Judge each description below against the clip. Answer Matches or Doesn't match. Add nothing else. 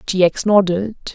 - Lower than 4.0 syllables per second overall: Doesn't match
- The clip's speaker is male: Doesn't match